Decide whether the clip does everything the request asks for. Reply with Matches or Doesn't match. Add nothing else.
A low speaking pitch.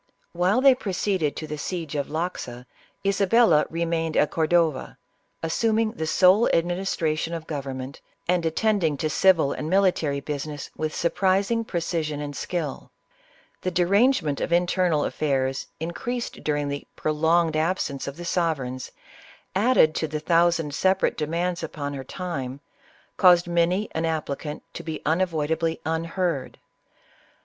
Doesn't match